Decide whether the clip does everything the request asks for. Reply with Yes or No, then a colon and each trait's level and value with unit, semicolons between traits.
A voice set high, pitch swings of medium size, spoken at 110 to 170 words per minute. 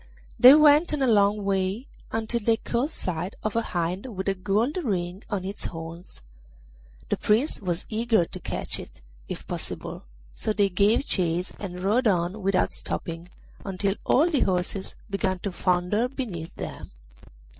Yes: high, 200 Hz; average, 4.1 semitones; average, 160 wpm